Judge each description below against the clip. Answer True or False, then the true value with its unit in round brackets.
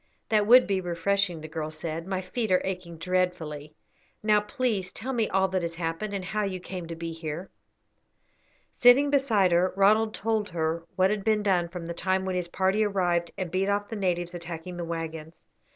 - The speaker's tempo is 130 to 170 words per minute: False (200 wpm)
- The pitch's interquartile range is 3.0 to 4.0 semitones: True (3.3 semitones)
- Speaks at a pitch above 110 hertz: True (185 Hz)